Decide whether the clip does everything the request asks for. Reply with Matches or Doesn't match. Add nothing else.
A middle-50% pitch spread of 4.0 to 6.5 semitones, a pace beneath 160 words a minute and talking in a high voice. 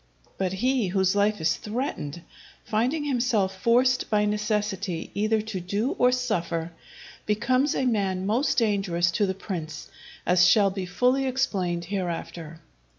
Matches